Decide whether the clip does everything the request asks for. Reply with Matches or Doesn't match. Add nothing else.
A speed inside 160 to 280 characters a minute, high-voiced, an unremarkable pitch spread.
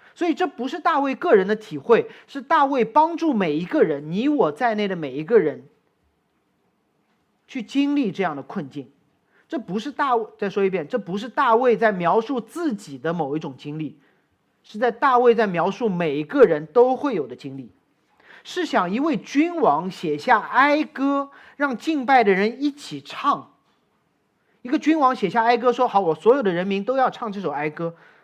Doesn't match